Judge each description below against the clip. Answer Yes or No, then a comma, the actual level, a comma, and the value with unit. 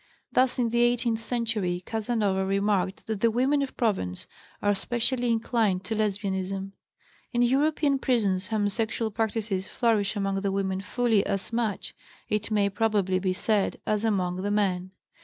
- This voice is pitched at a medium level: No, high, 210 Hz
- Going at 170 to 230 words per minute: No, average, 150 wpm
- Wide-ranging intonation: No, average, 3.2 semitones